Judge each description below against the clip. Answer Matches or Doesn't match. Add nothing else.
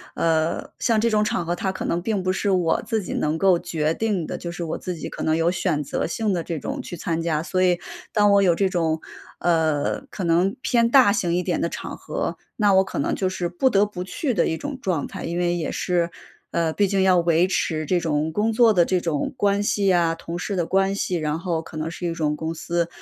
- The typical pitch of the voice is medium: Matches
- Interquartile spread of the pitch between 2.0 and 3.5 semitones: Matches